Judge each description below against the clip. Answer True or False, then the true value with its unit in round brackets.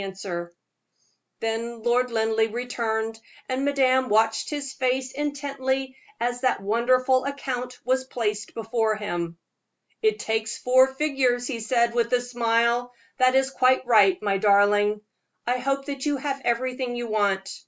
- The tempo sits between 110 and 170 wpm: True (140 wpm)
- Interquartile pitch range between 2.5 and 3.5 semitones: True (2.8 semitones)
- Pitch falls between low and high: False (245 Hz)